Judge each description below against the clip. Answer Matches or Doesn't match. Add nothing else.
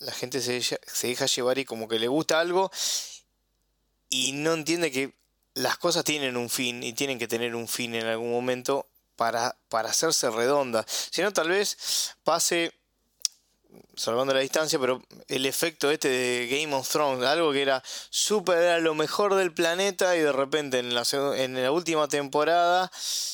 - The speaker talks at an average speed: Matches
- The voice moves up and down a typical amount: Matches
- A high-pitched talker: Doesn't match